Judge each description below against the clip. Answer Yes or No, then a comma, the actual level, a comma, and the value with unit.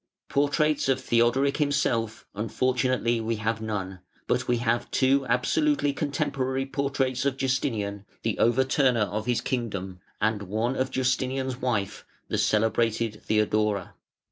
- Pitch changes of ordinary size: Yes, average, 3.4 semitones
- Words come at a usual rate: No, slow, 125 wpm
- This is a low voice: Yes, low, 120 Hz